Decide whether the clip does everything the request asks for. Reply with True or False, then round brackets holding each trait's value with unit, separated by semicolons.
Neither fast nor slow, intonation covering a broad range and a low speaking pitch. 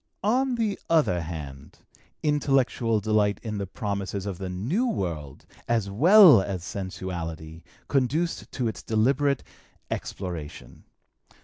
False (115 wpm; 7.3 semitones; 105 Hz)